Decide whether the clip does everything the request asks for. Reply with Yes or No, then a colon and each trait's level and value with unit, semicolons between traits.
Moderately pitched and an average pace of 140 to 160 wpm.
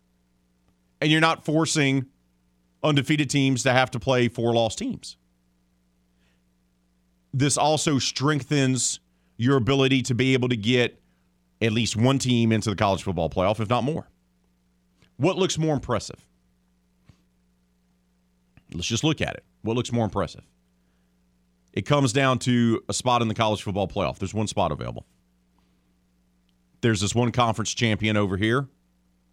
No: low, 100 Hz; average, 145 wpm